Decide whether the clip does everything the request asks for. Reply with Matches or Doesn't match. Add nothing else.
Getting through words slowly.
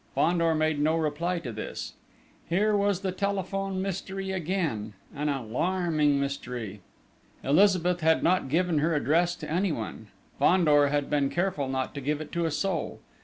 Doesn't match